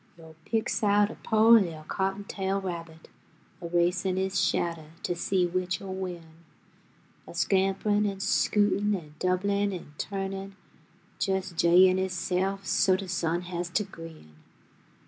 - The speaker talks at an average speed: No, slow, 130 wpm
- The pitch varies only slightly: Yes, narrow, 2.3 semitones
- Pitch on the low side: No, medium, 185 Hz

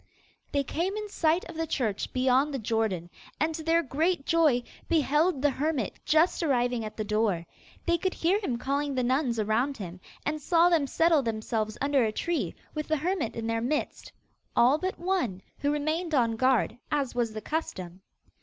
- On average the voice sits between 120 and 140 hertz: No, very high, 280 Hz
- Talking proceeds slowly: No, average, 185 wpm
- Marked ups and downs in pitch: Yes, wide, 6.0 semitones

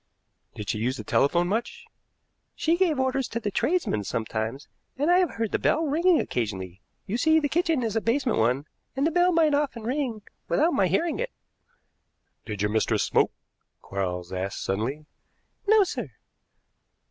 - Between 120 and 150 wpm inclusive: No, average, 170 wpm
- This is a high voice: Yes, high, 230 Hz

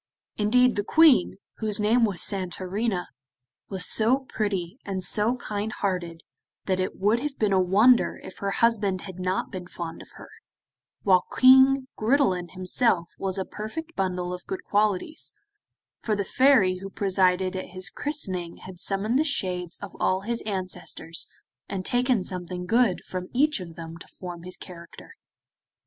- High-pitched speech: Yes, high, 195 Hz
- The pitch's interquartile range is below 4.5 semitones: Yes, average, 4.0 semitones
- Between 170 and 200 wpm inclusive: No, average, 160 wpm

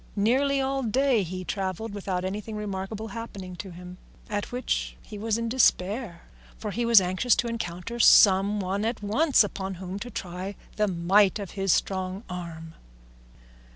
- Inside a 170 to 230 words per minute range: No, average, 160 wpm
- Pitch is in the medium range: No, high, 200 Hz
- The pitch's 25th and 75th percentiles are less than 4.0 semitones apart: Yes, average, 3.4 semitones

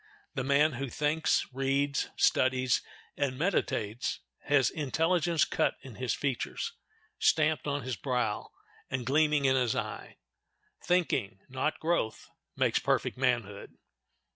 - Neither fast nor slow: No, slow, 120 wpm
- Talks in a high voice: No, low, 135 Hz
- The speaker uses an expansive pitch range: No, average, 3.2 semitones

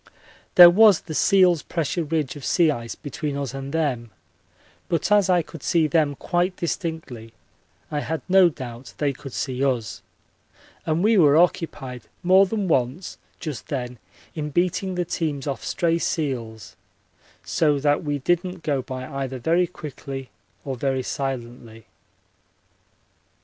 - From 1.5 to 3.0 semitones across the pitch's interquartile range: No, average, 4.6 semitones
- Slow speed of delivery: No, average, 145 wpm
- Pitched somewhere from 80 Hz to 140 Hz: No, medium, 150 Hz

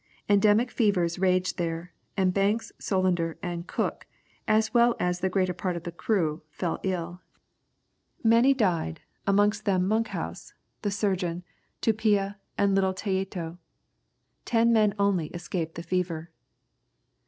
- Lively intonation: No, average, 3.0 semitones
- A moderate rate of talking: No, slow, 130 wpm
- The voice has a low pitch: No, high, 190 Hz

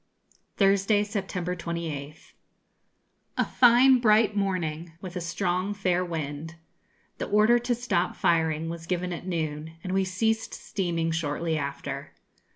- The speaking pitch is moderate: Yes, medium, 180 Hz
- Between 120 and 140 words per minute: Yes, slow, 135 wpm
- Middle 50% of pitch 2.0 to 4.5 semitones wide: Yes, average, 3.7 semitones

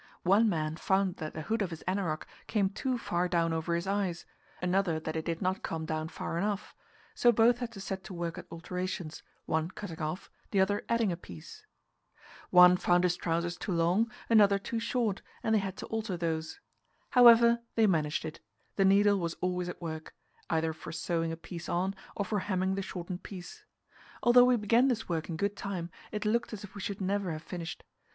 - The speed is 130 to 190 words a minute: No, fast, 205 wpm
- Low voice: No, medium, 185 Hz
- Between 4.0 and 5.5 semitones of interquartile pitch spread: No, average, 3.6 semitones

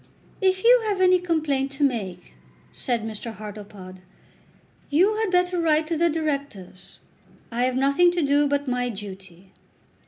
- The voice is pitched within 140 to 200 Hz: No, very high, 280 Hz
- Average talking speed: Yes, average, 150 wpm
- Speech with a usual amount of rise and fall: No, wide, 8.0 semitones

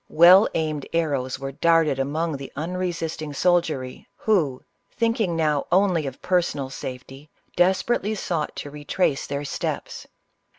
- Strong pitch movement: No, average, 4.2 semitones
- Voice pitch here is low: No, medium, 155 Hz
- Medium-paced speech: No, slow, 125 wpm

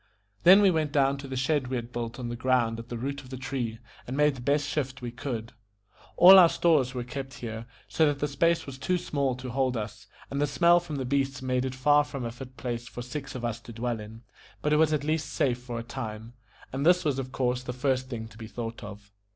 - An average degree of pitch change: Yes, average, 3.1 semitones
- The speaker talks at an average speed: No, fast, 255 wpm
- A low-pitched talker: Yes, low, 130 Hz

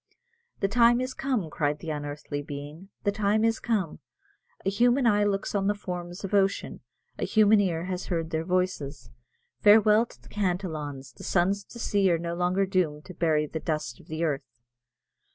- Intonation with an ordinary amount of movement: Yes, average, 4.6 semitones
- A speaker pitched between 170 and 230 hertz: Yes, medium, 185 Hz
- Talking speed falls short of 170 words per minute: No, average, 190 wpm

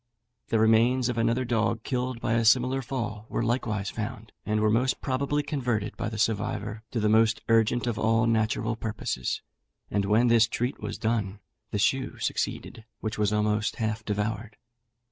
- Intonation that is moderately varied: No, narrow, 2.1 semitones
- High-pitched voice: No, low, 115 Hz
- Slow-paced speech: No, average, 170 wpm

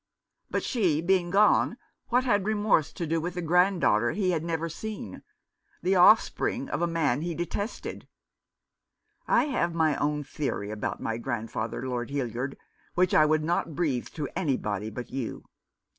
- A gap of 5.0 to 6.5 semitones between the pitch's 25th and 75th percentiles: Yes, wide, 5.4 semitones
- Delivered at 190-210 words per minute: No, average, 160 wpm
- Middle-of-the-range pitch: Yes, medium, 165 Hz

